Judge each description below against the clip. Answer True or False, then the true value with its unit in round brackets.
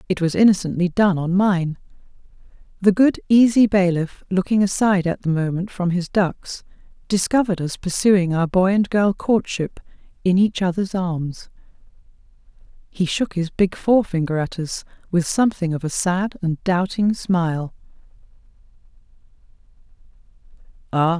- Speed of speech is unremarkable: False (125 wpm)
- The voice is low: False (185 Hz)